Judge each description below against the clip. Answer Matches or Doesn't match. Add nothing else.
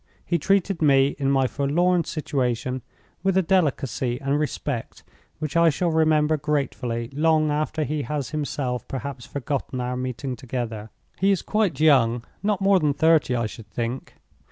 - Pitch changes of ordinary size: Matches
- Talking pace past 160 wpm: Doesn't match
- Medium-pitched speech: Matches